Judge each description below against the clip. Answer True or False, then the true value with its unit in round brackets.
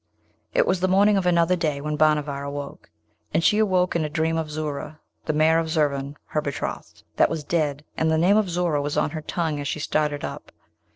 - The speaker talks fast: True (220 wpm)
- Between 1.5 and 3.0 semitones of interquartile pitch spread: True (2.5 semitones)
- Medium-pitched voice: True (155 Hz)